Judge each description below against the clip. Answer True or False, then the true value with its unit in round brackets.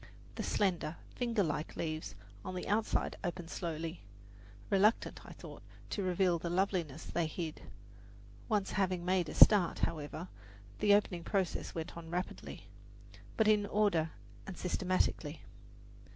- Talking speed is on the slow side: True (130 wpm)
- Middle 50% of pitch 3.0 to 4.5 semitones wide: True (3.4 semitones)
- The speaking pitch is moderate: True (180 Hz)